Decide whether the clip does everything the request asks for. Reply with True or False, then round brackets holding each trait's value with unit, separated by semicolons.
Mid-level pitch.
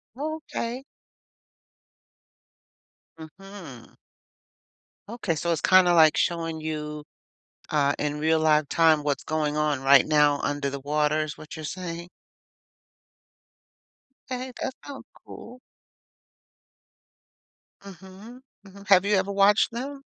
True (165 Hz)